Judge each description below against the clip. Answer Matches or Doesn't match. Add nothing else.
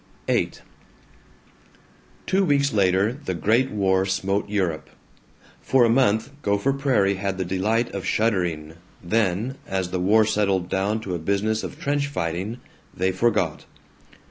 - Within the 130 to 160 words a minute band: Matches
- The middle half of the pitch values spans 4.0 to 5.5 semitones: Doesn't match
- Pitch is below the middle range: Matches